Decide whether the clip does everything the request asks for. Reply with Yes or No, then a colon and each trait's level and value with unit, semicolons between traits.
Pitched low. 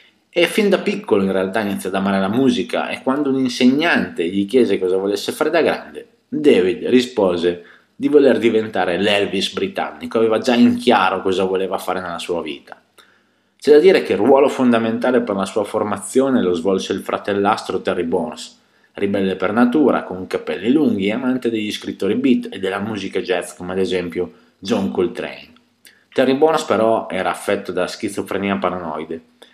Yes: low, 100 Hz